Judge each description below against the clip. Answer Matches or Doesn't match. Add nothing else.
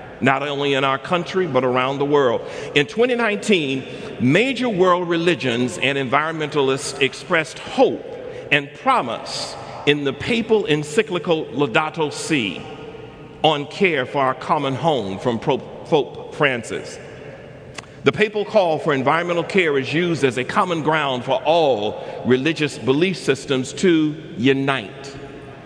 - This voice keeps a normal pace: Doesn't match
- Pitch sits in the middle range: Matches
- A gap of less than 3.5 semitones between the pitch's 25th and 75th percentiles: Doesn't match